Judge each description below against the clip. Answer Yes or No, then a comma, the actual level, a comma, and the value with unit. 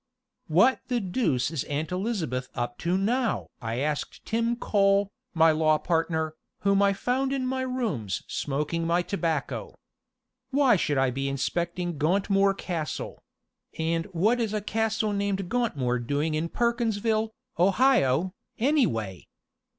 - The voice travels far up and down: Yes, wide, 6.5 semitones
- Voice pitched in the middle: Yes, medium, 180 Hz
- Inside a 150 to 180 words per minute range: No, slow, 135 wpm